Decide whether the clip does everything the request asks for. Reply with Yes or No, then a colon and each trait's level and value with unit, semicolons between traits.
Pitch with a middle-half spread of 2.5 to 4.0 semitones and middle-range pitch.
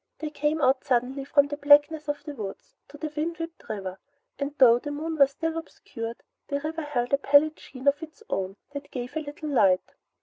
No: average, 3.0 semitones; very high, 285 Hz